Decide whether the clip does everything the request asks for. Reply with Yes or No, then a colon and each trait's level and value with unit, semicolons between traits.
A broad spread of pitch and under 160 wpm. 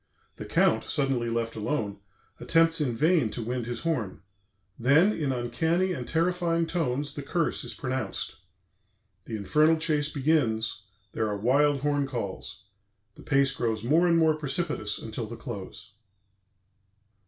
Yes: wide, 5.7 semitones; average, 140 wpm